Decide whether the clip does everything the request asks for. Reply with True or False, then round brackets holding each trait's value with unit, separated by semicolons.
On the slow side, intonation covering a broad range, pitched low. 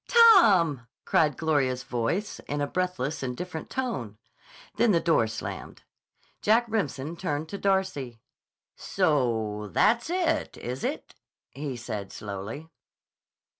False (120 wpm; 7.7 semitones; 150 Hz)